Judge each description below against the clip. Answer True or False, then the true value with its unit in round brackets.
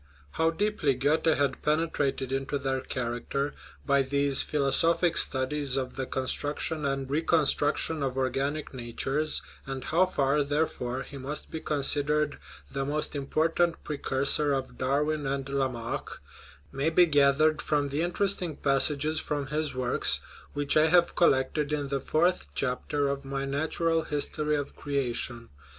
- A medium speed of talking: True (145 wpm)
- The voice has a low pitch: False (145 Hz)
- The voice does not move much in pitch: True (2.2 semitones)